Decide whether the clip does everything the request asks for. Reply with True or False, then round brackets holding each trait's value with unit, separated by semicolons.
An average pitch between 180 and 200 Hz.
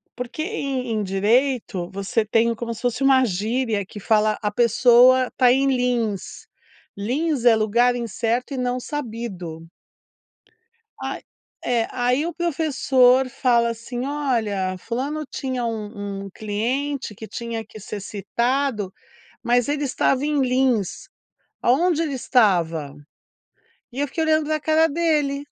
False (245 Hz)